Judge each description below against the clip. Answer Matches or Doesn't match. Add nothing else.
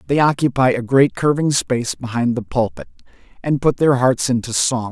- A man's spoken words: Matches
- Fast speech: Doesn't match